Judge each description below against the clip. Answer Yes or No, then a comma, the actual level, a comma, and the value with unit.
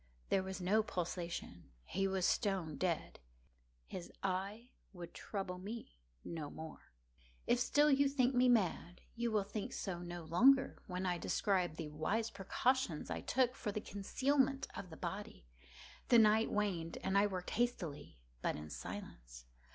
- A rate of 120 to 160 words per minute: Yes, average, 155 wpm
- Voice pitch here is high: Yes, high, 195 Hz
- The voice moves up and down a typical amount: Yes, average, 4.9 semitones